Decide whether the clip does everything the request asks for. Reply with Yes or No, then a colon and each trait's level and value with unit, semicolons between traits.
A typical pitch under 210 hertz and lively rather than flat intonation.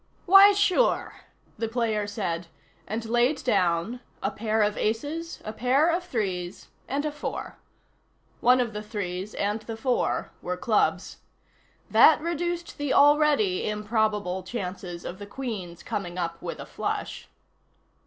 No: high, 220 Hz; wide, 6.1 semitones